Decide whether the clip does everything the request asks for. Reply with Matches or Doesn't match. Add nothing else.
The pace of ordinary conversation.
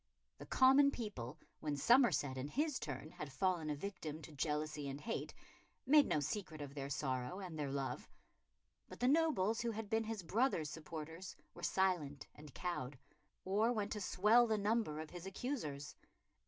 Matches